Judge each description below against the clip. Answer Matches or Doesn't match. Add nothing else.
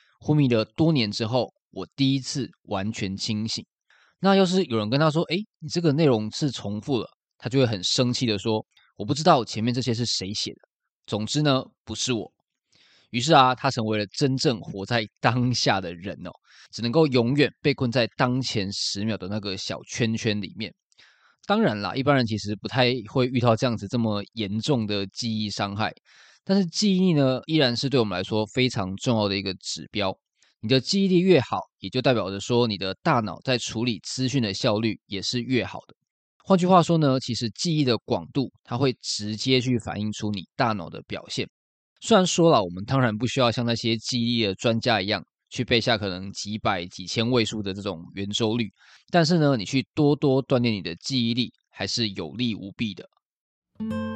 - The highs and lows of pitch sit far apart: Doesn't match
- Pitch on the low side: Matches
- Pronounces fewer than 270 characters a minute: Doesn't match